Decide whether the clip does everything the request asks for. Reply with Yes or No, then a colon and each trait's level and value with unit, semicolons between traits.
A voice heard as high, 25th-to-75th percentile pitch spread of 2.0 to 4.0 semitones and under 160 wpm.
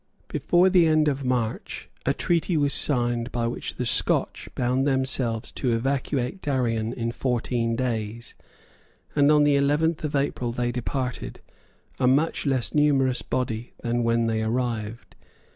No: low, 125 Hz; average, 3.4 semitones; average, 145 wpm